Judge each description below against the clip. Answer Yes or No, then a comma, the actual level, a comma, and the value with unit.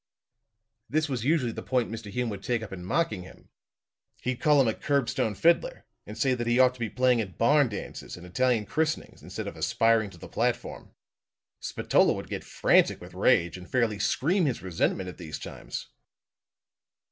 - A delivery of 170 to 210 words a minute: Yes, average, 185 wpm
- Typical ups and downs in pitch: Yes, average, 4.9 semitones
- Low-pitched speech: Yes, low, 120 Hz